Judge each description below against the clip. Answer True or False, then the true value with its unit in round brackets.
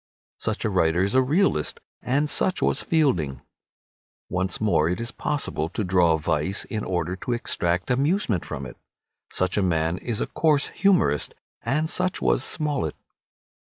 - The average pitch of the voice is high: False (100 Hz)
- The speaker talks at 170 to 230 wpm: False (160 wpm)